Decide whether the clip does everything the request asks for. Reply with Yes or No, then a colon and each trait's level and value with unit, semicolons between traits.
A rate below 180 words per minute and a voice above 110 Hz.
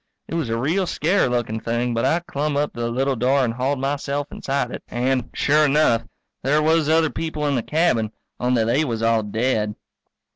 No: fast, 205 wpm; low, 135 Hz